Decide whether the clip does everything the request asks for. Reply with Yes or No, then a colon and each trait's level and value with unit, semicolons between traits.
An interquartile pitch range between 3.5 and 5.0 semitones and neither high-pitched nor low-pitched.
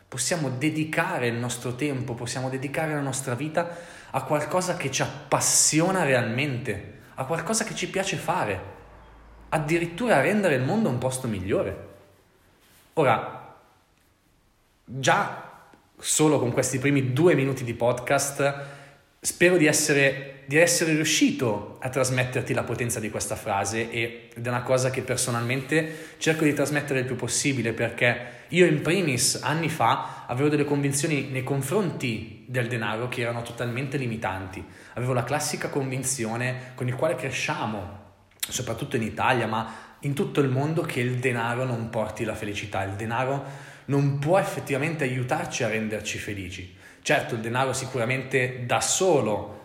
No: average, 3.9 semitones; low, 130 Hz